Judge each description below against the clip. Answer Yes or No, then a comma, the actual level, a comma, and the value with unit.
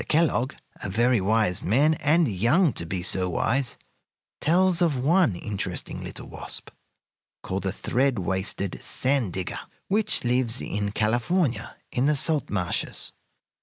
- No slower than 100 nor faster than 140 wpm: Yes, slow, 135 wpm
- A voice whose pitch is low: Yes, low, 120 Hz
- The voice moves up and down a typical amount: No, wide, 7.2 semitones